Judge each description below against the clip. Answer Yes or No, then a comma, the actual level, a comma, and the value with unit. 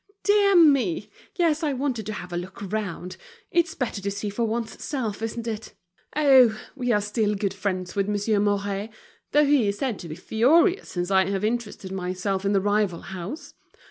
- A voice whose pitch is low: No, high, 210 Hz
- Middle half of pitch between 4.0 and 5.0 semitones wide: Yes, average, 4.4 semitones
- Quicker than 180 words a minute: Yes, average, 190 wpm